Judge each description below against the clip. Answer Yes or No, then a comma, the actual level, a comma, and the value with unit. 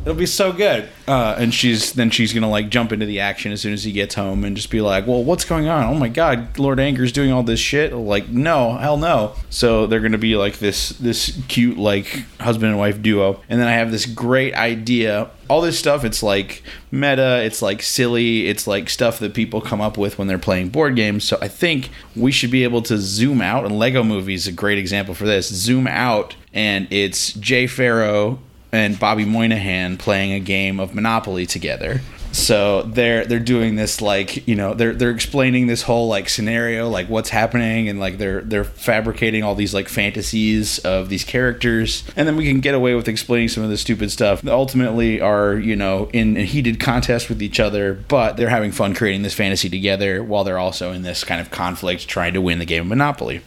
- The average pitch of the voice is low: Yes, low, 110 Hz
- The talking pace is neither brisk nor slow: No, fast, 220 wpm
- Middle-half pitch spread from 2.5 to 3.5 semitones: Yes, average, 3.2 semitones